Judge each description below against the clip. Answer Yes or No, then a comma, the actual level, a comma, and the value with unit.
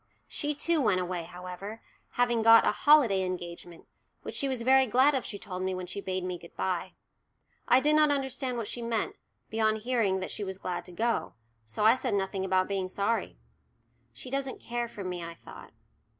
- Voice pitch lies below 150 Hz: No, high, 210 Hz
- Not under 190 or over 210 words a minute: Yes, average, 200 wpm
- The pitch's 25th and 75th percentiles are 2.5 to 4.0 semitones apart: No, average, 5.0 semitones